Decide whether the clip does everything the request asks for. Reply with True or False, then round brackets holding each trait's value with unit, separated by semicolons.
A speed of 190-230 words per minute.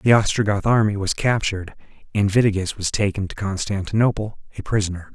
False (150 wpm)